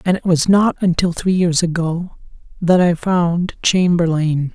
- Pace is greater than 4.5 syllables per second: No, 4.3 syllables/s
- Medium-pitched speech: Yes, medium, 175 Hz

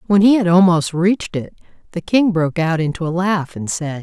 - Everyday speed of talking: No, fast, 225 wpm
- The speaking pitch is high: No, medium, 175 Hz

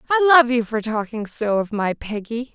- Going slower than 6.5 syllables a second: Yes, 4.8 syllables/s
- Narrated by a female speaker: Yes, female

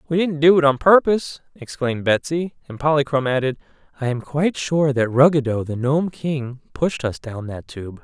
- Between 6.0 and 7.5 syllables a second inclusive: No, 5.2 syllables/s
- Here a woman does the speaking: No, male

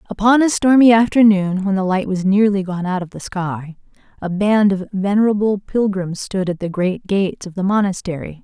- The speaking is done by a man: No, female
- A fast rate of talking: No, average, 190 wpm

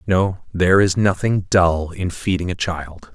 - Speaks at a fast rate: No, average, 170 wpm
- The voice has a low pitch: Yes, very low, 90 Hz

